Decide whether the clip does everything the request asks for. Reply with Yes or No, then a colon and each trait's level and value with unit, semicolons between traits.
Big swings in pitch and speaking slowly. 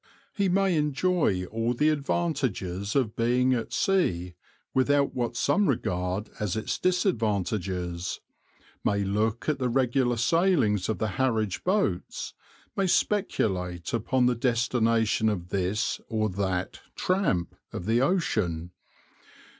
Yes: wide, 6.3 semitones; slow, 120 wpm